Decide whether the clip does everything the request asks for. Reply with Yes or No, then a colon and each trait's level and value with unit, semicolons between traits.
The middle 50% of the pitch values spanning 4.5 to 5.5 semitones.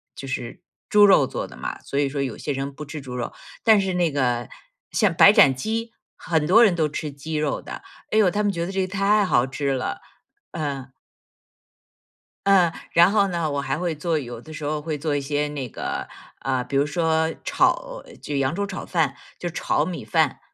Yes: average, 4.9 semitones